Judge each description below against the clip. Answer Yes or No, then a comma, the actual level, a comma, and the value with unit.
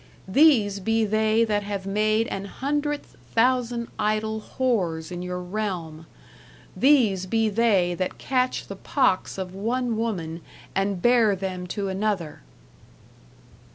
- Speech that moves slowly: Yes, slow, 130 wpm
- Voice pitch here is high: Yes, high, 210 Hz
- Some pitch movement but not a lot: Yes, average, 3.5 semitones